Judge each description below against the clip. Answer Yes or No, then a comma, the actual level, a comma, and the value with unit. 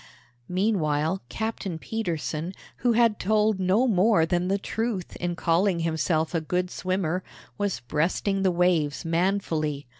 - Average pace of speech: No, slow, 130 wpm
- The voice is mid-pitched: Yes, medium, 180 Hz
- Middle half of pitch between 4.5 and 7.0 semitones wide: No, average, 3.7 semitones